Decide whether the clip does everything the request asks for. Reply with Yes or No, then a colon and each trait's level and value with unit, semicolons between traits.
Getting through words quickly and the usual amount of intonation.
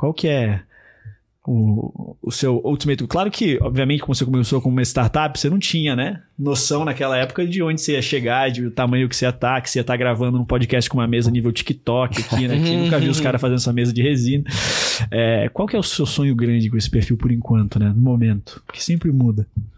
Yes: fast, 235 wpm; average, 3.3 semitones